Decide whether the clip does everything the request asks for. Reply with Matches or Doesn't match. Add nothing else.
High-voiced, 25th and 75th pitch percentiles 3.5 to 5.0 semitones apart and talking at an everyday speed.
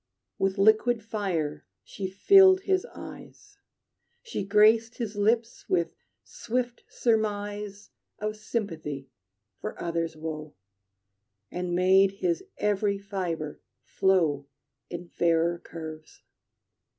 Doesn't match